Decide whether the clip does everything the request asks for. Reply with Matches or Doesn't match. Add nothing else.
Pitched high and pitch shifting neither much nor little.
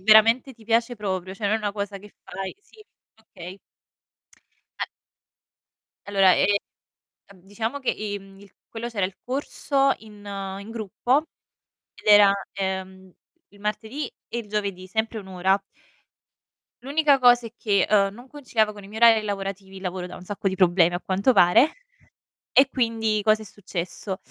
Matches